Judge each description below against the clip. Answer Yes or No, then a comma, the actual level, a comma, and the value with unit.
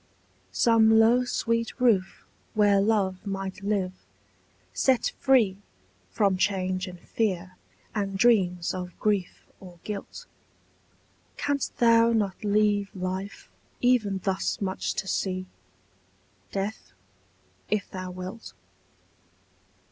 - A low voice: No, high, 200 Hz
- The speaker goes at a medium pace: No, slow, 100 wpm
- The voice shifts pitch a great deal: No, average, 3.0 semitones